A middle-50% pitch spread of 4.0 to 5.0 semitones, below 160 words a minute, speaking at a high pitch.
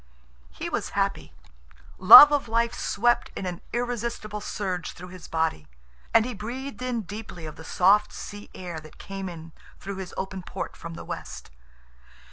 No: average, 4.6 semitones; average, 165 wpm; high, 195 Hz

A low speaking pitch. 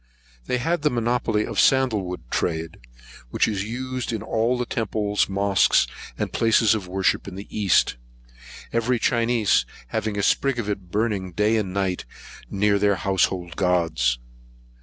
Yes: low, 105 Hz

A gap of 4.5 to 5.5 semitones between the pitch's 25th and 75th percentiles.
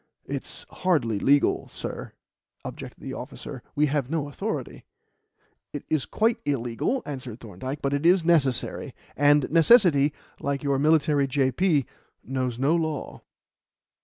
No: average, 3.3 semitones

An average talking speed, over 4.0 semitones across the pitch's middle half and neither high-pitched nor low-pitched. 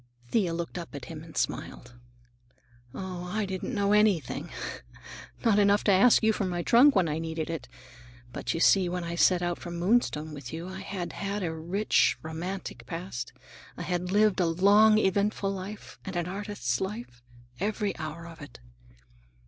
No: average, 175 wpm; average, 3.5 semitones; medium, 180 Hz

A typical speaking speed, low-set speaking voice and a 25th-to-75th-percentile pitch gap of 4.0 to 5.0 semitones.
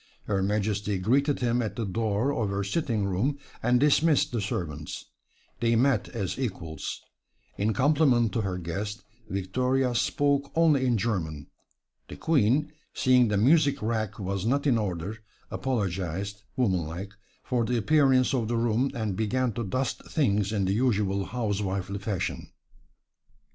Yes: average, 145 wpm; low, 110 Hz; average, 4.6 semitones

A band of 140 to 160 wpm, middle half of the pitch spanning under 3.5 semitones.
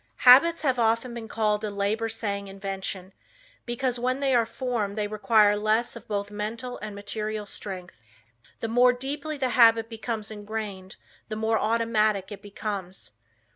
Yes: average, 155 wpm; narrow, 2.6 semitones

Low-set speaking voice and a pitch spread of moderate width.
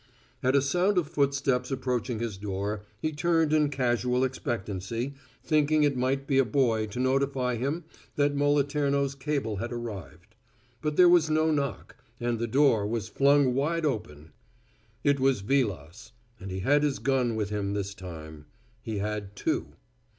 Yes: low, 130 Hz; average, 4.9 semitones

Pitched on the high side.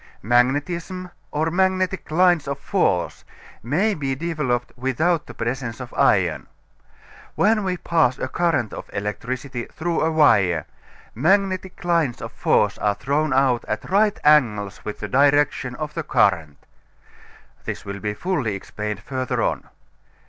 No: medium, 140 Hz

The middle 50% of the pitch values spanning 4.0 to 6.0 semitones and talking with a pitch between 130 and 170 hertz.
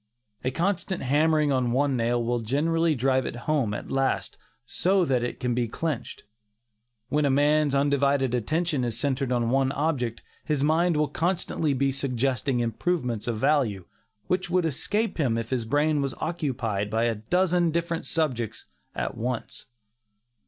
Yes: average, 4.5 semitones; medium, 140 Hz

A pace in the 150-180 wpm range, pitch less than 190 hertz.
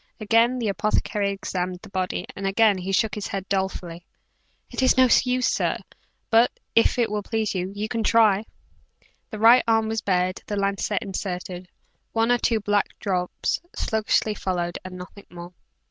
No: average, 160 wpm; high, 205 Hz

